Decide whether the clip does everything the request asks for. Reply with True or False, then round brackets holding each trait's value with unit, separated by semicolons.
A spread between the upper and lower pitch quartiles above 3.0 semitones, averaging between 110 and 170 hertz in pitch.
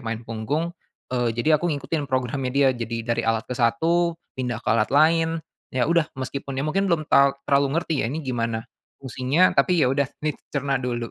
True (4.6 semitones; 135 Hz)